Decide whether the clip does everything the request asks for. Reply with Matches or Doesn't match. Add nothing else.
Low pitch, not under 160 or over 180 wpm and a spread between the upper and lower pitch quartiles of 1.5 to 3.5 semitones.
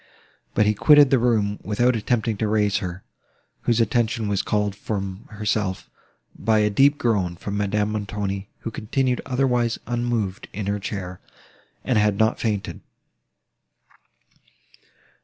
Doesn't match